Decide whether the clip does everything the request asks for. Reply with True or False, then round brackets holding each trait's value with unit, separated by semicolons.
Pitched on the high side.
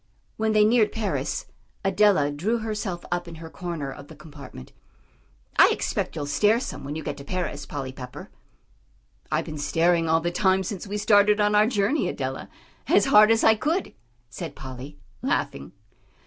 False (180 Hz)